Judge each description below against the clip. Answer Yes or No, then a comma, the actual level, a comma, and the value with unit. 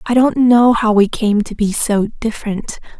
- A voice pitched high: Yes, high, 220 Hz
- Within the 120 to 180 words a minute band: No, average, 200 wpm